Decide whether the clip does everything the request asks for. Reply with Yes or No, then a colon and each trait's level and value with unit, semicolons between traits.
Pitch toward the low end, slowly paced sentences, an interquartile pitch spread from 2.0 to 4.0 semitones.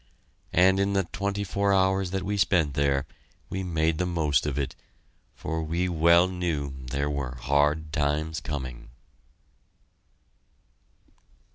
No: very low, 80 Hz; slow, 130 wpm; average, 4.6 semitones